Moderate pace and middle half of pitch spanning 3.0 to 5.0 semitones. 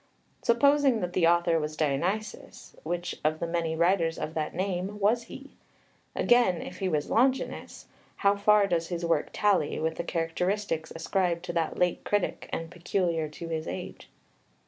Yes: average, 165 wpm; average, 3.6 semitones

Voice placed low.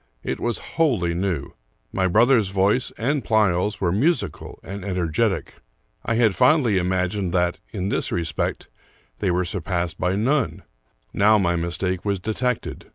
Yes: very low, 95 Hz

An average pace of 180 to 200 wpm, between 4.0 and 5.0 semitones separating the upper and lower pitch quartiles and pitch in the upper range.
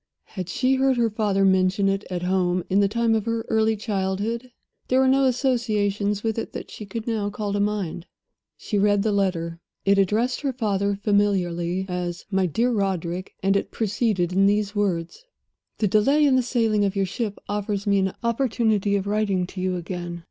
No: average, 190 wpm; average, 2.9 semitones; high, 205 Hz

